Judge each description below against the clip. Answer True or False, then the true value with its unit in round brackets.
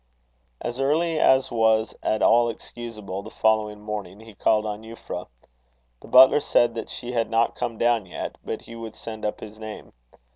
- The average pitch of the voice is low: True (115 Hz)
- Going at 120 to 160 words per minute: False (180 wpm)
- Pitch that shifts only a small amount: True (1.9 semitones)